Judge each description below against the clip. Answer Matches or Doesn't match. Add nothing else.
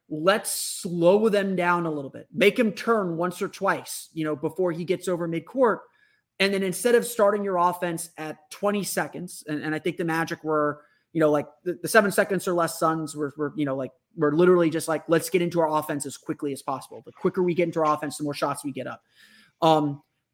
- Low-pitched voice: Doesn't match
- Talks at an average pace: Doesn't match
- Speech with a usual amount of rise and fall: Matches